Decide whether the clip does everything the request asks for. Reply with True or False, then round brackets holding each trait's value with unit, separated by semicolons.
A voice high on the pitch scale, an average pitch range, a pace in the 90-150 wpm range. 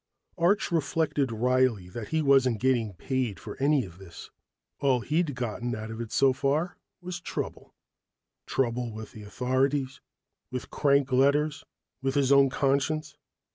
False (130 Hz; 3.3 semitones; 145 wpm)